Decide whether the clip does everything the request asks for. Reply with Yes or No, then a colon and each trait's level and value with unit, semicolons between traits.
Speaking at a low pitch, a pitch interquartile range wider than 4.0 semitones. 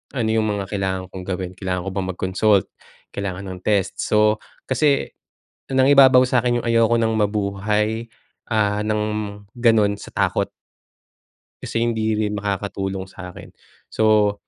No: low, 105 Hz; narrow, 2.5 semitones